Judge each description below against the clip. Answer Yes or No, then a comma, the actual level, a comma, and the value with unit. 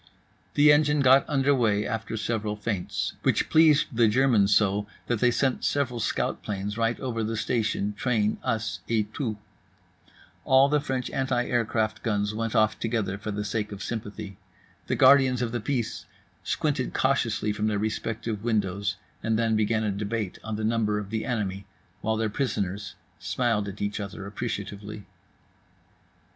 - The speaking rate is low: No, average, 160 wpm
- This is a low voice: Yes, low, 110 Hz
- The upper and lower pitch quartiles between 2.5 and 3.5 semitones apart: Yes, average, 2.8 semitones